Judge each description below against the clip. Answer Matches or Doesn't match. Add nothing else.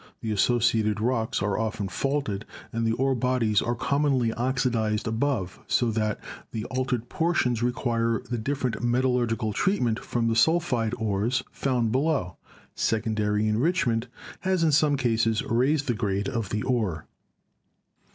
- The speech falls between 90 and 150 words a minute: Matches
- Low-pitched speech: Matches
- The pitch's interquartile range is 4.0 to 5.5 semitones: Doesn't match